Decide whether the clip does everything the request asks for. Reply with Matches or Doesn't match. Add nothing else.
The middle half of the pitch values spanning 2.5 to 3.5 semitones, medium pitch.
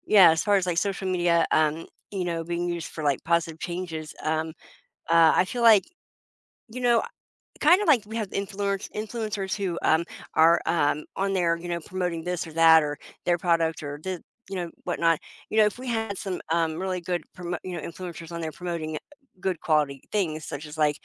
Matches